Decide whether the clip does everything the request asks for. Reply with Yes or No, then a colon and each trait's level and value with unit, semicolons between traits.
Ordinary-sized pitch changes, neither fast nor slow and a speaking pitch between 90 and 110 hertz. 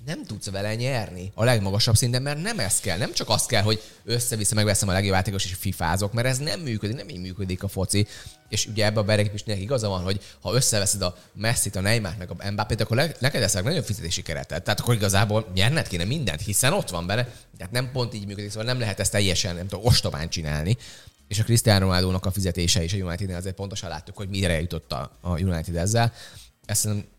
No: average, 3.6 semitones; fast, 225 wpm; low, 105 Hz